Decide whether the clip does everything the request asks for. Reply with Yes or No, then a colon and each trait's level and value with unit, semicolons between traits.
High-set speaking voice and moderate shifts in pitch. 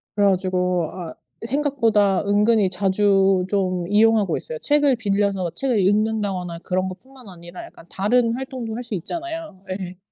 Yes: high, 205 Hz; average, 4.1 semitones